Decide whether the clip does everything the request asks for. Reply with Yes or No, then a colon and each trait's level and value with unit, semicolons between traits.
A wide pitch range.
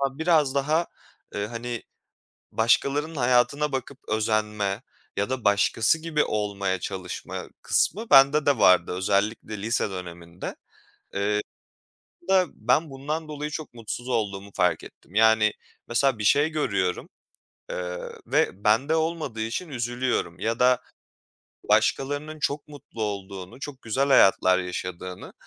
Yes: wide, 5.9 semitones